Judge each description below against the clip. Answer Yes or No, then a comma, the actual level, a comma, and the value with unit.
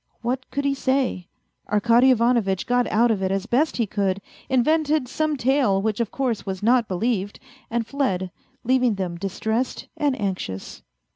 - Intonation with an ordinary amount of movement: Yes, average, 4.9 semitones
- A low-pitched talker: No, high, 235 Hz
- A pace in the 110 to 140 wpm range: No, average, 160 wpm